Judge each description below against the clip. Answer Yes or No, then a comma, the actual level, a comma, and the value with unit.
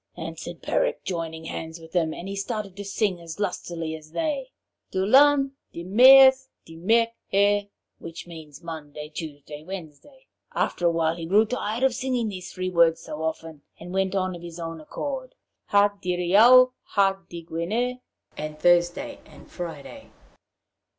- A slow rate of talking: No, average, 145 wpm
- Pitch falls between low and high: Yes, medium, 180 Hz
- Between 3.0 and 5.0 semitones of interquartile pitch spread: No, wide, 5.4 semitones